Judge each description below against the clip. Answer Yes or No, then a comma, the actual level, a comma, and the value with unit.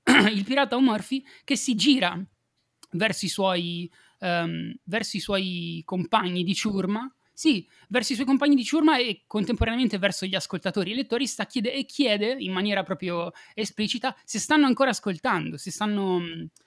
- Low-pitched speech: No, high, 215 Hz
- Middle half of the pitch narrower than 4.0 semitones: No, wide, 5.6 semitones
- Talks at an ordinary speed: Yes, average, 150 wpm